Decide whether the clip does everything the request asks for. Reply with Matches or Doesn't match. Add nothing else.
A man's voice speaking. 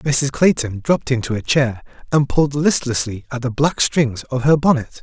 Matches